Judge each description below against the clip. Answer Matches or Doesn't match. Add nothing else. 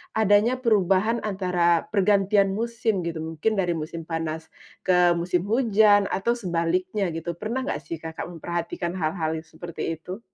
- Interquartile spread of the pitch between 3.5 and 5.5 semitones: Matches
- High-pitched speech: Doesn't match